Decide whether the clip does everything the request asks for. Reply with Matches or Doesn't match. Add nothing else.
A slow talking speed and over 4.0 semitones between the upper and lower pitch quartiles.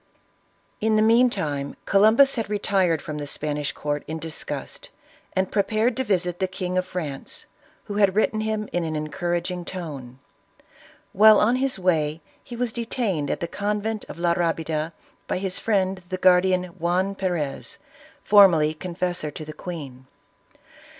Doesn't match